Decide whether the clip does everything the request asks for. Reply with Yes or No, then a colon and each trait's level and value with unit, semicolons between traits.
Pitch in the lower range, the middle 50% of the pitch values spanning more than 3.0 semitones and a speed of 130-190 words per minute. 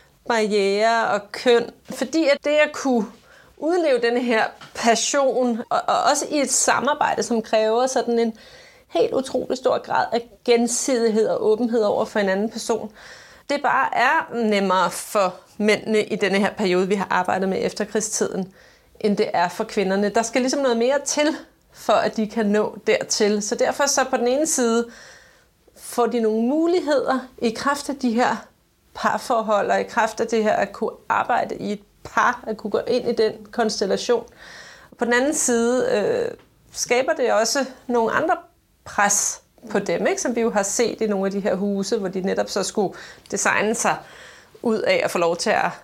No: high, 230 Hz; average, 3.6 semitones; average, 185 wpm